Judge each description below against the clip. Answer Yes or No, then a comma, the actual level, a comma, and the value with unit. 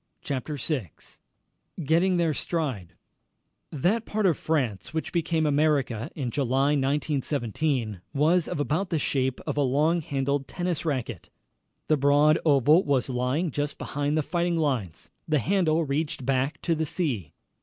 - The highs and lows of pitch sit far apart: No, average, 3.2 semitones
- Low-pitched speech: No, medium, 145 Hz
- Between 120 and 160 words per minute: Yes, average, 145 wpm